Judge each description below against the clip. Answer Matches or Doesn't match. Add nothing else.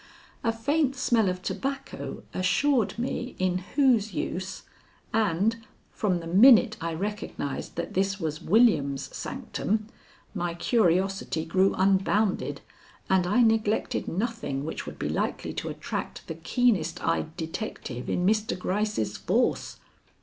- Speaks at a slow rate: Matches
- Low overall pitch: Doesn't match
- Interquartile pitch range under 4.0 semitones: Doesn't match